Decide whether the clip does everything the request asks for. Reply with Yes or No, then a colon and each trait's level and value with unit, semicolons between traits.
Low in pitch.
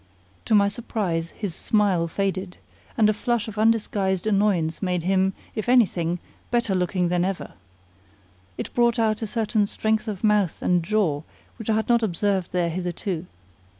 No: high, 200 Hz